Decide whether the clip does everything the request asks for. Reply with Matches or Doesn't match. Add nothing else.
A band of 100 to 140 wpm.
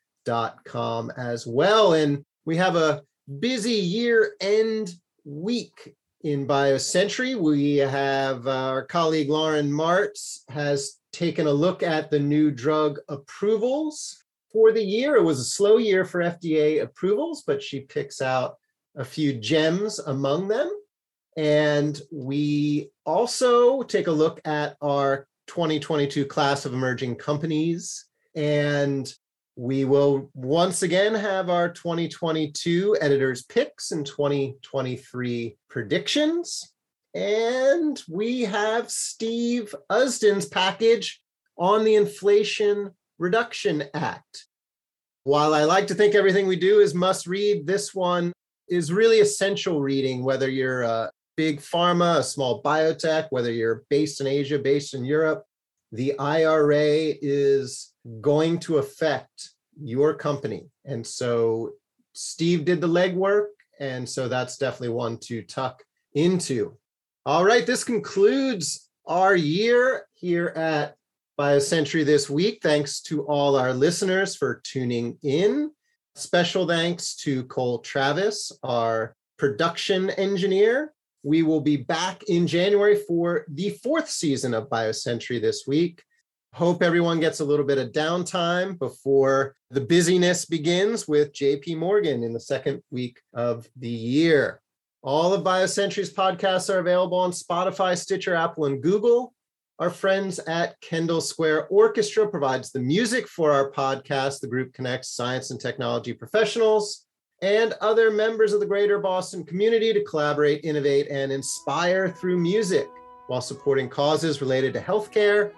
Matches